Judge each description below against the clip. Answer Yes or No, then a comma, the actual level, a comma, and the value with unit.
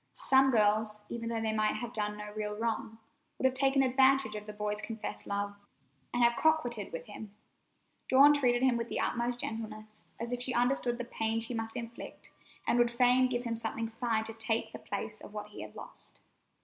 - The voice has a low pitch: No, high, 230 Hz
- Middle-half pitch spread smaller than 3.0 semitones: Yes, narrow, 2.4 semitones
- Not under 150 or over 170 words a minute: No, fast, 205 wpm